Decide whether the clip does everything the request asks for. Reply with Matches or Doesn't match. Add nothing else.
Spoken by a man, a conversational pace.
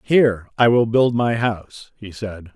Matches